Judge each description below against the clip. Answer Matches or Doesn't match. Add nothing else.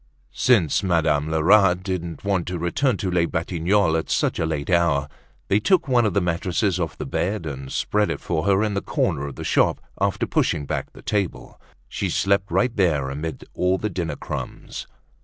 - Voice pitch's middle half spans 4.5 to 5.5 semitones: Doesn't match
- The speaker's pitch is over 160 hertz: Doesn't match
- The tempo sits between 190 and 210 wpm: Matches